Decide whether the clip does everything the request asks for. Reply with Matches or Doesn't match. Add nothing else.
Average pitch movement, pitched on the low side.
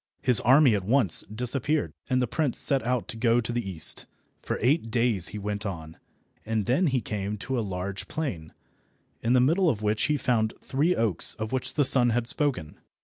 Matches